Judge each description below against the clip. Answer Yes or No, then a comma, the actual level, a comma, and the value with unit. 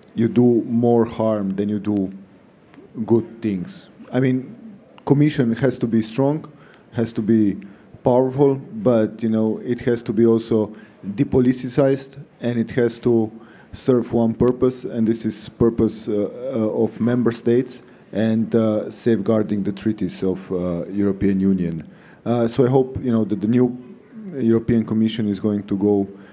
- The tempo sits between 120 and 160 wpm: Yes, average, 155 wpm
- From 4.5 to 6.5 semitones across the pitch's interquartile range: No, average, 2.7 semitones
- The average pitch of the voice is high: No, low, 115 Hz